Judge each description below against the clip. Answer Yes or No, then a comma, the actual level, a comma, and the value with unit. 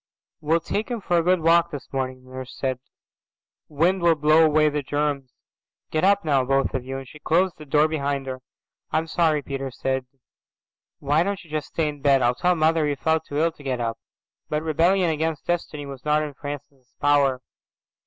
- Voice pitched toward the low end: No, medium, 150 Hz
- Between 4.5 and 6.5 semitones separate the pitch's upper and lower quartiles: No, average, 3.1 semitones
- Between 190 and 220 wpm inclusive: Yes, average, 200 wpm